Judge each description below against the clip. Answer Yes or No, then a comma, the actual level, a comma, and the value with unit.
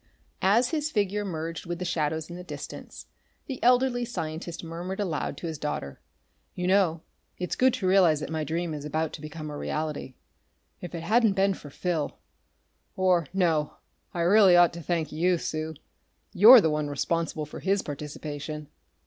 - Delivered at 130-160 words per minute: No, average, 175 wpm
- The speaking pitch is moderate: Yes, medium, 170 Hz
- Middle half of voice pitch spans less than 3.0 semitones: No, average, 3.7 semitones